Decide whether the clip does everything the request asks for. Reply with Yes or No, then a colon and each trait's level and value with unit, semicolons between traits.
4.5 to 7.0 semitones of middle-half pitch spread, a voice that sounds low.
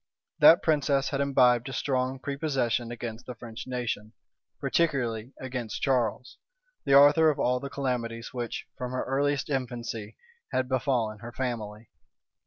No: average, 2.7 semitones; low, 125 Hz